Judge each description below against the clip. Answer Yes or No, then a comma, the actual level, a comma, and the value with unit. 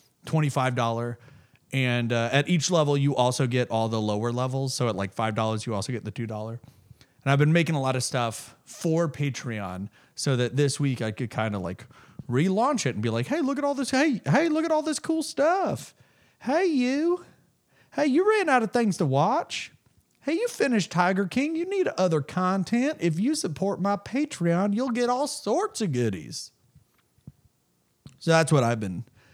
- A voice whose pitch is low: No, medium, 145 Hz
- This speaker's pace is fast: No, average, 190 wpm